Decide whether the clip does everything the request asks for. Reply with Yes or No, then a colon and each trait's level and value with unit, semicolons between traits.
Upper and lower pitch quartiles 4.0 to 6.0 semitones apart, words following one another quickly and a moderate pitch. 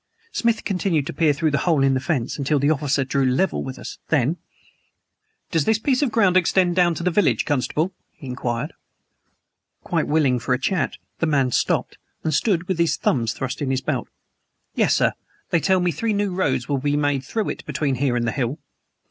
Yes: average, 5.2 semitones; fast, 210 wpm; medium, 150 Hz